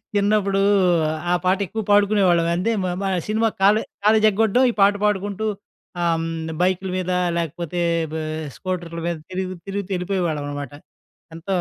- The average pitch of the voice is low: No, high, 190 Hz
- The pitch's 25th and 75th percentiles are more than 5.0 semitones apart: No, average, 2.9 semitones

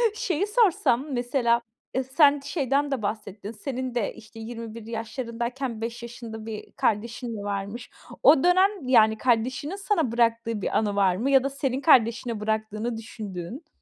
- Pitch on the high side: Yes, high, 235 Hz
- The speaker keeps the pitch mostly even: No, average, 3.7 semitones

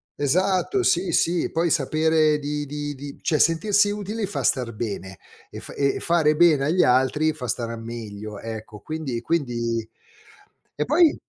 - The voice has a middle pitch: Yes, medium, 150 Hz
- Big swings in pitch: Yes, wide, 6.1 semitones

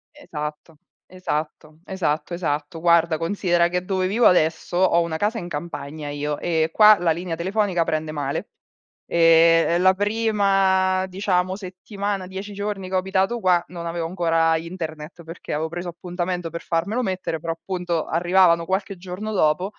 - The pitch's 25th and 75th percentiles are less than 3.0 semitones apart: Yes, narrow, 2.5 semitones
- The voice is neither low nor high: Yes, medium, 175 Hz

